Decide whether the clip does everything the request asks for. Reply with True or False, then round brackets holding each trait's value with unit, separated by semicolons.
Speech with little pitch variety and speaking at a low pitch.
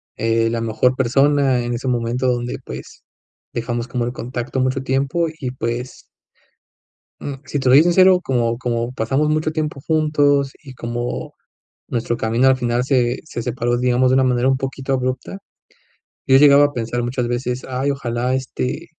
True (2.2 semitones; 130 Hz)